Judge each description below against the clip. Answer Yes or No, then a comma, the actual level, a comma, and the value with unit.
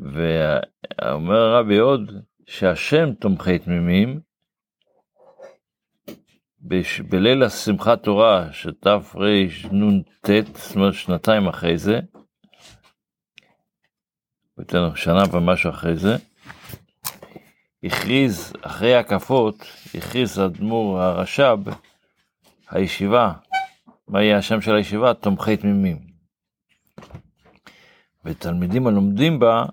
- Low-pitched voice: Yes, low, 100 Hz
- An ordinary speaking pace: No, slow, 80 wpm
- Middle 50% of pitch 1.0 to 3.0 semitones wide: No, average, 3.7 semitones